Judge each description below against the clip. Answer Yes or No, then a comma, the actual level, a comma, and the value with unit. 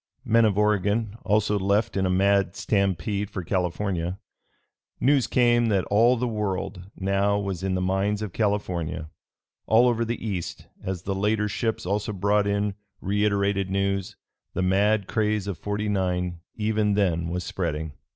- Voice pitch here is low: Yes, low, 100 Hz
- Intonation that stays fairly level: Yes, narrow, 2.1 semitones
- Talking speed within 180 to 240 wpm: No, average, 150 wpm